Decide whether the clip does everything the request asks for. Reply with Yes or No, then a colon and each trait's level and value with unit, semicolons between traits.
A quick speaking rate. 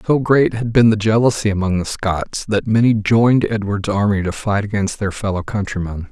No: average, 195 wpm